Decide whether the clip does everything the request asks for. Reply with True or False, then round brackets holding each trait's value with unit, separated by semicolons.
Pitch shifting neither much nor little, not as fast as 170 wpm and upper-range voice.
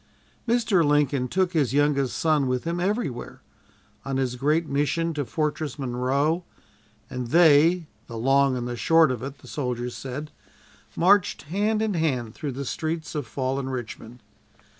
False (4.4 semitones; 155 wpm; 145 Hz)